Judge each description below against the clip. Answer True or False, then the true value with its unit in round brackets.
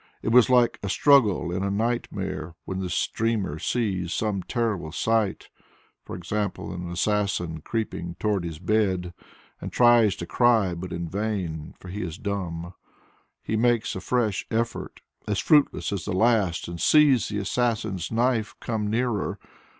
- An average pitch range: True (4.3 semitones)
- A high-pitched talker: False (100 Hz)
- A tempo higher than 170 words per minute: False (150 wpm)